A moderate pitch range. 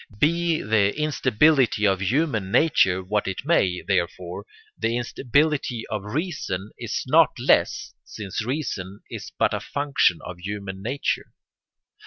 No: wide, 7.0 semitones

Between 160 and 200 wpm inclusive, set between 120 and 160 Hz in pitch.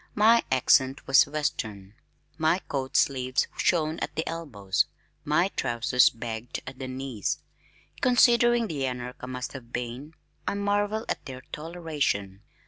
No: slow, 135 wpm; low, 135 Hz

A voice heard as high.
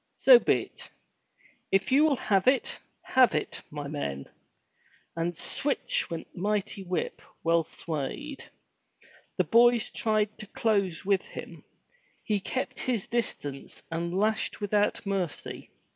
Yes: high, 200 Hz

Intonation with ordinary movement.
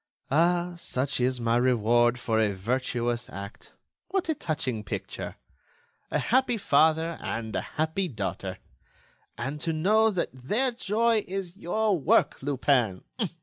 No: wide, 8.1 semitones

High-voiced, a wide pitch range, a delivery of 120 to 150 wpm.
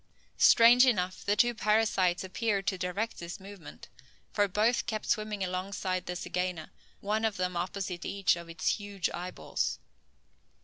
No: high, 195 Hz; average, 2.9 semitones; average, 145 wpm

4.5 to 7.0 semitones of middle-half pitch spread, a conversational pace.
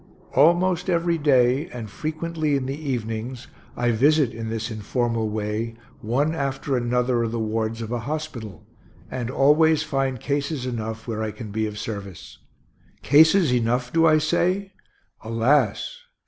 Yes: average, 5.3 semitones; average, 150 wpm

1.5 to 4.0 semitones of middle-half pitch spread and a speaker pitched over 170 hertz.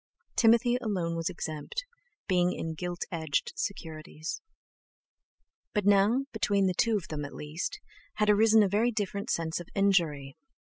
No: average, 4.7 semitones; high, 190 Hz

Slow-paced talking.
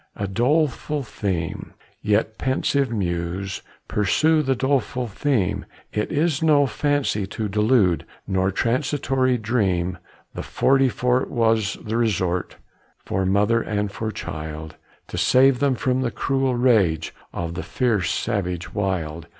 Yes: slow, 130 wpm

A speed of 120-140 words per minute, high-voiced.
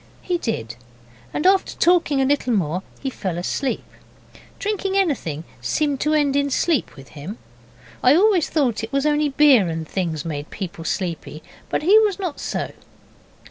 No: average, 165 wpm; very high, 270 Hz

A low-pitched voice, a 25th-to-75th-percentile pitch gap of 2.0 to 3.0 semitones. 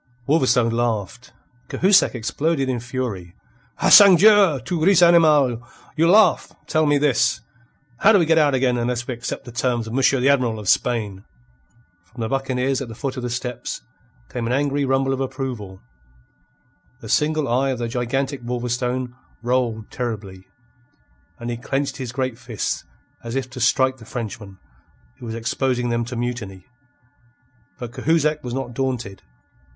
Yes: low, 125 Hz; narrow, 2.6 semitones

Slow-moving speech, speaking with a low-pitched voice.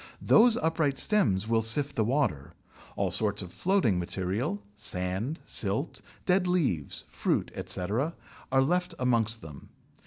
Yes: slow, 130 wpm; low, 120 Hz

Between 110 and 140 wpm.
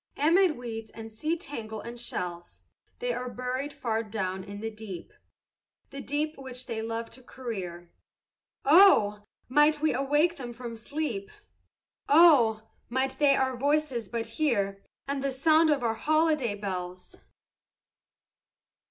Yes: slow, 135 wpm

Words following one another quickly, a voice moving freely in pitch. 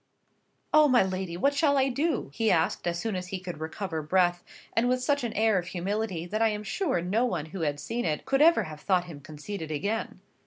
Yes: fast, 230 wpm; wide, 5.9 semitones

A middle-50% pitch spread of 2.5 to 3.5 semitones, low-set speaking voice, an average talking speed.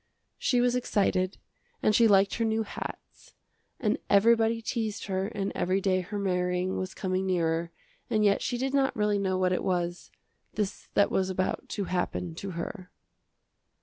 No: average, 3.0 semitones; high, 195 Hz; average, 170 wpm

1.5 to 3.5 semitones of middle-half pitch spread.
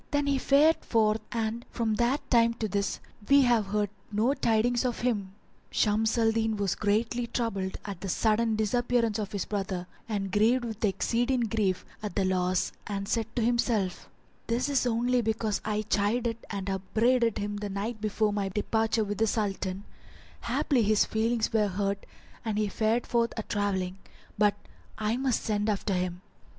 Yes: narrow, 2.5 semitones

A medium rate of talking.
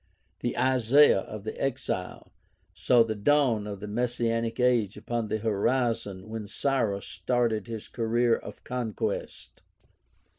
No: slow, 125 wpm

